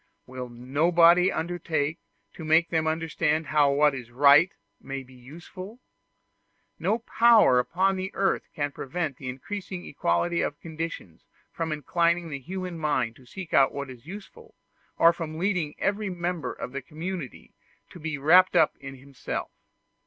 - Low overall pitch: No, medium, 160 Hz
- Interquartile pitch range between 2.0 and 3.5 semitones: No, average, 4.3 semitones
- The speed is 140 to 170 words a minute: Yes, average, 150 wpm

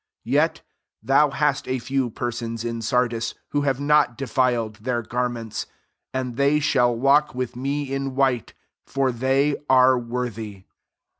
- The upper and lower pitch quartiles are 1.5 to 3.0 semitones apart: Yes, narrow, 2.5 semitones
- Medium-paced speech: Yes, average, 150 wpm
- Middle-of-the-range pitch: No, low, 125 Hz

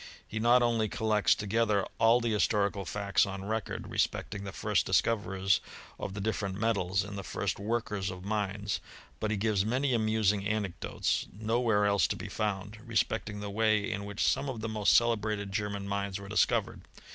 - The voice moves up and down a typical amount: No, narrow, 1.8 semitones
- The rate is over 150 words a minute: Yes, average, 180 wpm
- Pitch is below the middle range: Yes, low, 105 Hz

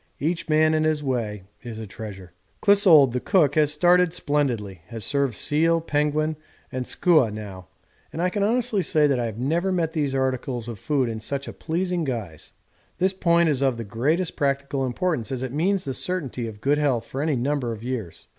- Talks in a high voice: No, medium, 140 Hz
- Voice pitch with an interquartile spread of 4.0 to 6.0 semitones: Yes, wide, 5.5 semitones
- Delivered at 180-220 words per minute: Yes, average, 200 wpm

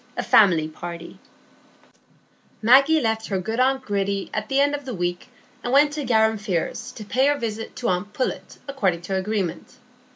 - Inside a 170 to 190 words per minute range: Yes, average, 175 wpm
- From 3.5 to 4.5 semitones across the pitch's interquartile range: No, wide, 5.4 semitones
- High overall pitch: Yes, high, 220 Hz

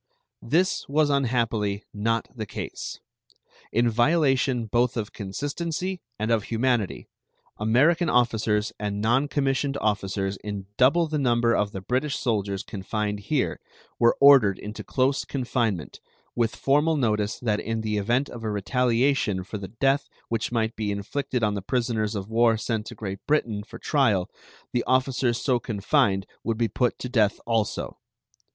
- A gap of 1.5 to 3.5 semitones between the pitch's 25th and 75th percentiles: No, average, 3.9 semitones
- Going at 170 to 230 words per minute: No, average, 155 wpm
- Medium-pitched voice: No, low, 115 Hz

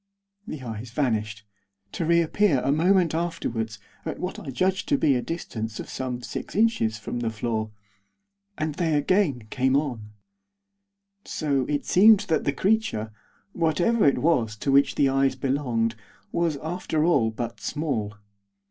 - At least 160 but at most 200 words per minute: No, average, 150 wpm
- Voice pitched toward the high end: No, medium, 140 Hz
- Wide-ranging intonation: Yes, wide, 6.3 semitones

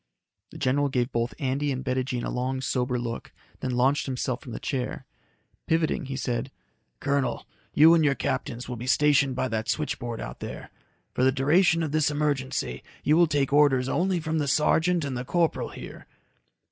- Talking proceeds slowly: No, average, 185 wpm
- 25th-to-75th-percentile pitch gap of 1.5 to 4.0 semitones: Yes, average, 2.9 semitones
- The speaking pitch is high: No, low, 135 Hz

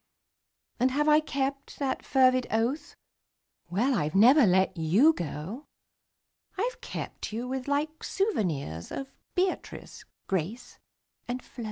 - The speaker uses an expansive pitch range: Yes, wide, 6.9 semitones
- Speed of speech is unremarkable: No, slow, 125 wpm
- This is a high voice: Yes, very high, 255 Hz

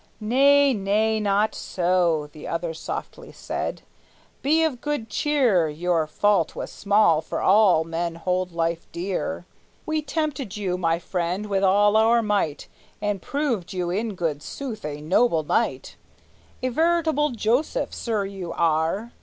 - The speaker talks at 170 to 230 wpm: No, average, 145 wpm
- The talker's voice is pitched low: No, high, 200 Hz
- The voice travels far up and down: Yes, wide, 5.7 semitones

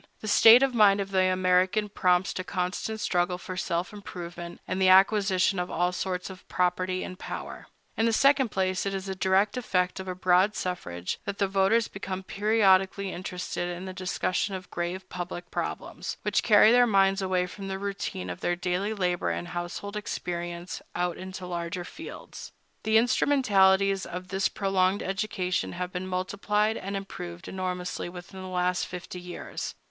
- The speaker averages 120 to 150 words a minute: No, average, 175 wpm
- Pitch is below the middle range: No, medium, 185 Hz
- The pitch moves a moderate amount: No, narrow, 1.7 semitones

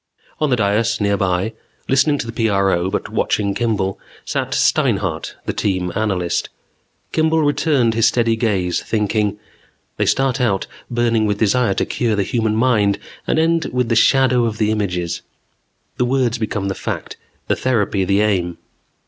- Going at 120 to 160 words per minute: Yes, average, 155 wpm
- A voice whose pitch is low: Yes, low, 110 Hz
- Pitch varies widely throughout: No, average, 3.7 semitones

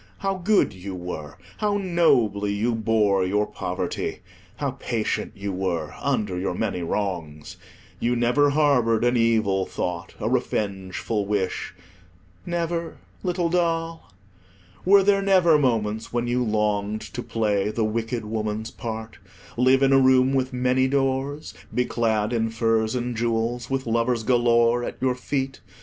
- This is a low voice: Yes, low, 115 Hz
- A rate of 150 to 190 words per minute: No, average, 140 wpm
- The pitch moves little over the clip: No, average, 4.3 semitones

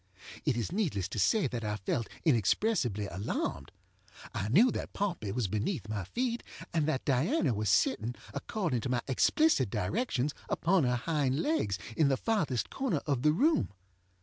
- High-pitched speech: No, low, 130 Hz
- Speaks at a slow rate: No, average, 165 wpm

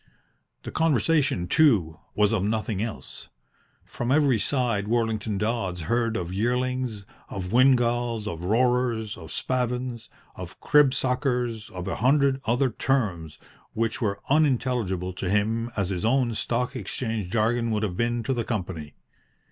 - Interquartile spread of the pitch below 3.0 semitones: No, average, 3.8 semitones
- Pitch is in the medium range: No, low, 115 Hz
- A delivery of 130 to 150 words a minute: Yes, average, 140 wpm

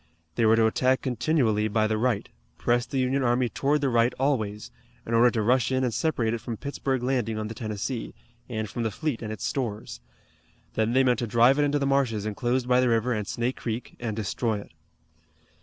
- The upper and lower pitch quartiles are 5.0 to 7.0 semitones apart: No, average, 3.0 semitones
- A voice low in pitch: Yes, low, 120 Hz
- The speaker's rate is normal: No, fast, 215 wpm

